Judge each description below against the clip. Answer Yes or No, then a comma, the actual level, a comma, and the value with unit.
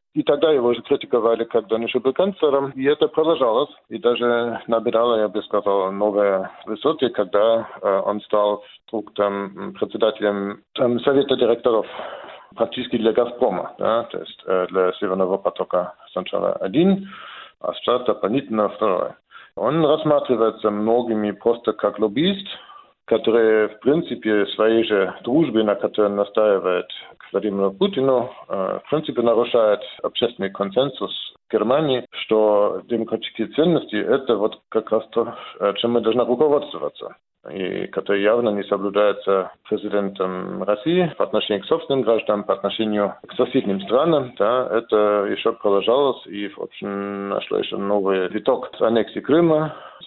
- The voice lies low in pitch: Yes, low, 110 Hz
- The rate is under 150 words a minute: Yes, average, 135 wpm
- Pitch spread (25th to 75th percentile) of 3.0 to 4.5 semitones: Yes, average, 3.6 semitones